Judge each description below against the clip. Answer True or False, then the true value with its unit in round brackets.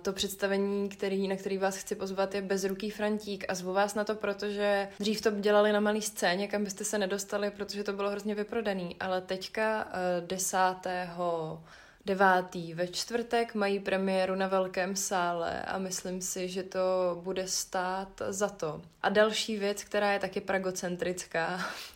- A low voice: False (195 Hz)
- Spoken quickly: False (160 wpm)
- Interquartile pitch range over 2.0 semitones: False (1.7 semitones)